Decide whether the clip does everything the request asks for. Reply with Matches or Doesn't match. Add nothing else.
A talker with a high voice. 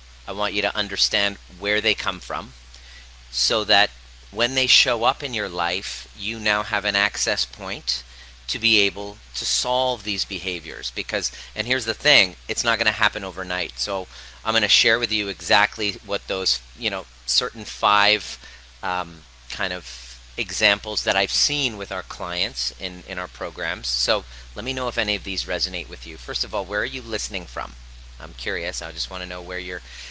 Doesn't match